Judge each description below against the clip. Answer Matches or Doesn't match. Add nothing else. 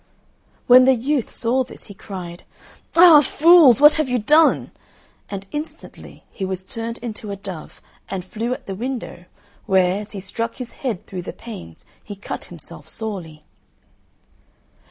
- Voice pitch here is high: Matches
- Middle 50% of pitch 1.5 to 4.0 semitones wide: Doesn't match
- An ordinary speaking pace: Matches